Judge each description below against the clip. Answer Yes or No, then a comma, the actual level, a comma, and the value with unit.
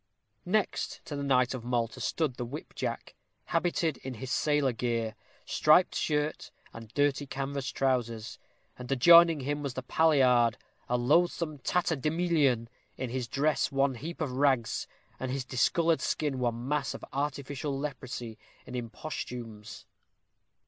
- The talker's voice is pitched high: No, low, 135 Hz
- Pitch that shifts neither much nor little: Yes, average, 3.4 semitones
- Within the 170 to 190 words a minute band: No, slow, 135 wpm